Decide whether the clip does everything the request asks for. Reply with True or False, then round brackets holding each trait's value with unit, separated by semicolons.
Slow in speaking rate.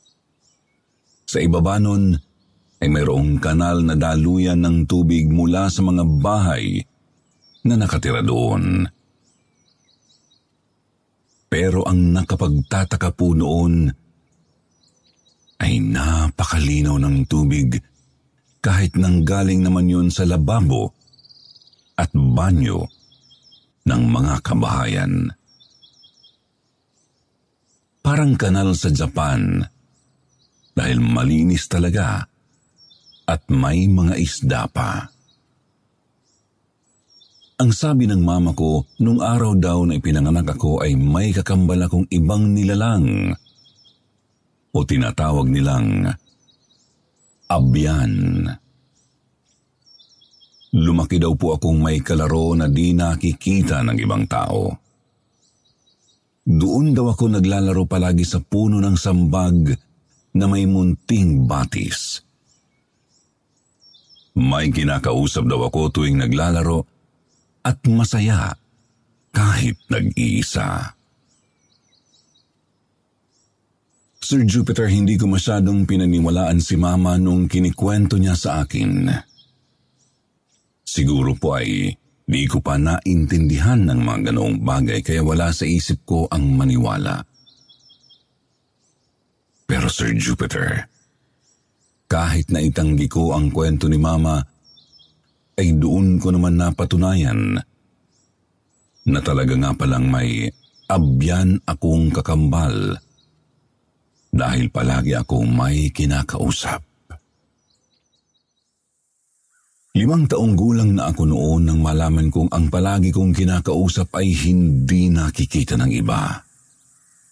True (95 wpm)